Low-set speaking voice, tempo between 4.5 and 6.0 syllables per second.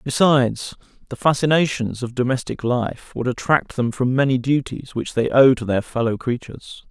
Yes: low, 130 Hz; 5.0 syllables/s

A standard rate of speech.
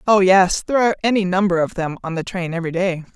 No: fast, 245 wpm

